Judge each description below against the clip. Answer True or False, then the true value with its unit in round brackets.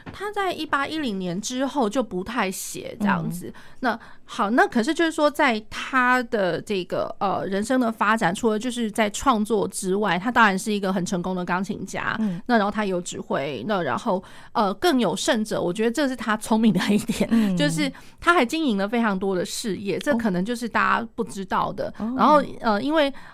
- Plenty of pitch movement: False (4.6 semitones)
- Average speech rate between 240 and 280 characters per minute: False (290 characters per minute)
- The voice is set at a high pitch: True (220 Hz)